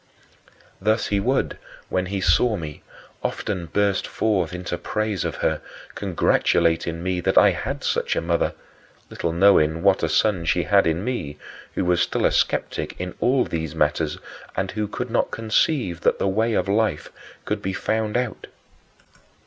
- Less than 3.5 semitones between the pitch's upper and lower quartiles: No, average, 4.2 semitones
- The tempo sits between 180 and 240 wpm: No, average, 170 wpm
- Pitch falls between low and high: No, very low, 95 Hz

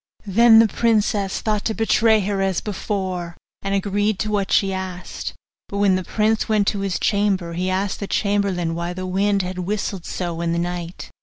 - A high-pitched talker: Yes, high, 195 Hz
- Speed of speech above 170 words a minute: Yes, average, 190 wpm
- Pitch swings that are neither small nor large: No, narrow, 2.2 semitones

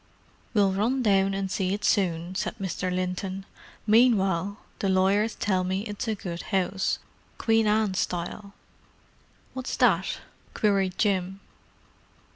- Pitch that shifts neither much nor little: No, narrow, 2.1 semitones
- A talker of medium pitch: No, high, 195 Hz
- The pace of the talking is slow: Yes, slow, 125 wpm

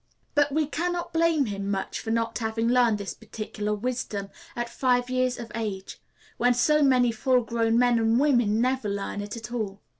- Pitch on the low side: No, high, 235 Hz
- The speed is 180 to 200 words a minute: Yes, average, 190 wpm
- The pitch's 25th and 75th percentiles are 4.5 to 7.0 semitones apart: No, average, 2.9 semitones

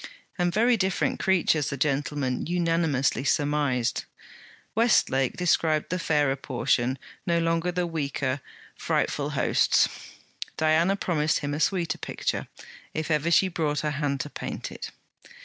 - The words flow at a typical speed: No, slow, 130 wpm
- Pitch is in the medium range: Yes, medium, 155 Hz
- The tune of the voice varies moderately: Yes, average, 3.3 semitones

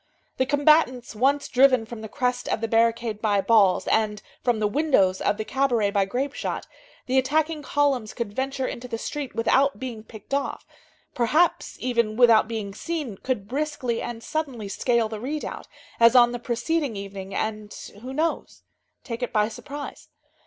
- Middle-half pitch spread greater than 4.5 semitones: No, average, 4.0 semitones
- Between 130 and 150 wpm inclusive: No, average, 170 wpm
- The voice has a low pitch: No, high, 240 Hz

